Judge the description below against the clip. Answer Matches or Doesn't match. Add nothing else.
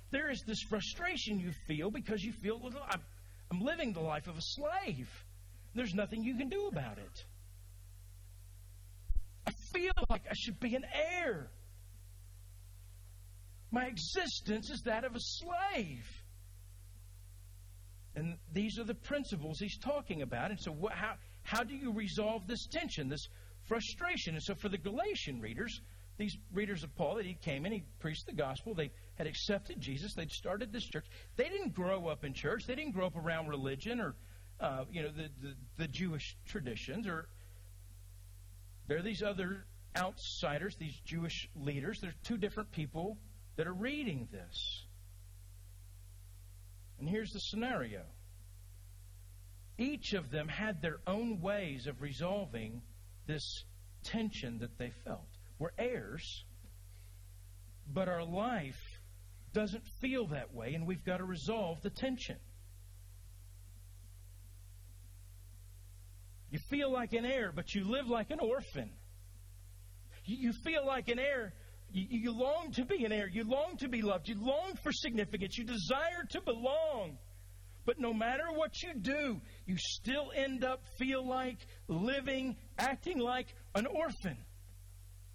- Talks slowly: Doesn't match